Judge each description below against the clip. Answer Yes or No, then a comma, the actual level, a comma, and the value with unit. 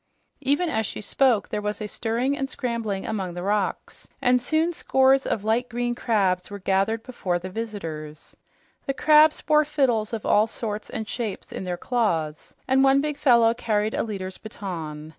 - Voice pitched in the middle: No, high, 220 Hz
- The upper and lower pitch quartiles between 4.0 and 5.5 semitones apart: Yes, average, 4.8 semitones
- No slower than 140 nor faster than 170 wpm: No, average, 180 wpm